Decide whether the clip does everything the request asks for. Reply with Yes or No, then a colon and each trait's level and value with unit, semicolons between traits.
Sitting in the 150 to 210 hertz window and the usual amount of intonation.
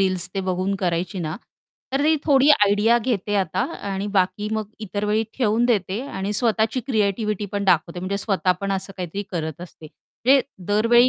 Yes: high, 200 Hz; average, 3.1 semitones